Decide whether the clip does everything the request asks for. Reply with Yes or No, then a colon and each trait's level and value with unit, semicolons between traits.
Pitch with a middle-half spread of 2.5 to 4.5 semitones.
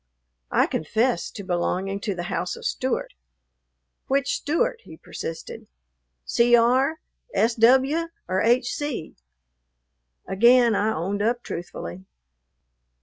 No: average, 5.3 semitones